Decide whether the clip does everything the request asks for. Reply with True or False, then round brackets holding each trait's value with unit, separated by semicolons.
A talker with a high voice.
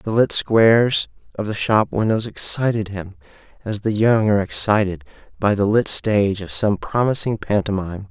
False (105 Hz)